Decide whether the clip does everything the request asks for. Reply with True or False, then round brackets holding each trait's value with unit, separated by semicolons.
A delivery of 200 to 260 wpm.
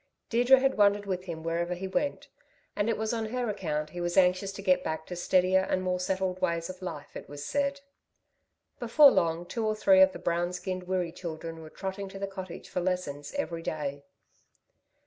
True (205 wpm)